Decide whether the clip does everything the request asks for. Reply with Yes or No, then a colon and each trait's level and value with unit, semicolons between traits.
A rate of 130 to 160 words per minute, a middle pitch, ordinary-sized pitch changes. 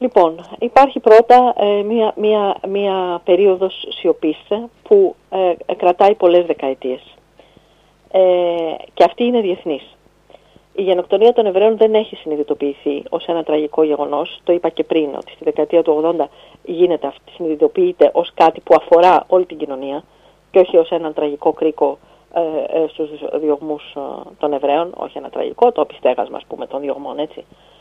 Yes: average, 150 wpm; medium, 175 Hz; average, 4.6 semitones